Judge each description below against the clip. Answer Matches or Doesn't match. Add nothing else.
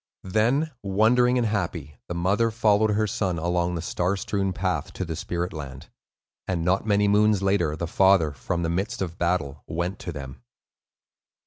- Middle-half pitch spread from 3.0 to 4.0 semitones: Matches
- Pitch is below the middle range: Matches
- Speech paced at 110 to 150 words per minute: Doesn't match